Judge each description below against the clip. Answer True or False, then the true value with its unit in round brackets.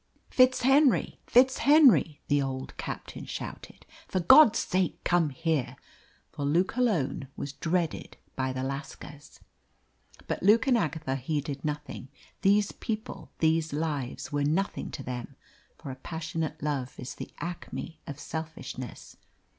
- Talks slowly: True (130 wpm)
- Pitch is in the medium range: True (160 Hz)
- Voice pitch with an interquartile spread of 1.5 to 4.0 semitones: False (5.3 semitones)